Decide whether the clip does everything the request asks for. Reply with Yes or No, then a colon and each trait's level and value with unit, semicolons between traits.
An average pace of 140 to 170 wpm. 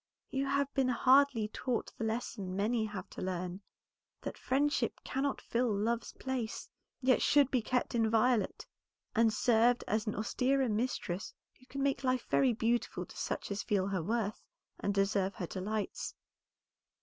Yes: average, 155 wpm